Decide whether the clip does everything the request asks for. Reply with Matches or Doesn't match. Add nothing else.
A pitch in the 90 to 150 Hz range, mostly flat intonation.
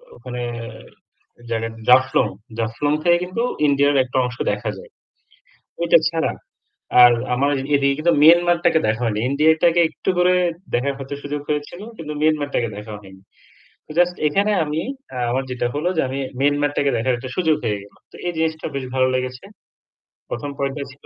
Doesn't match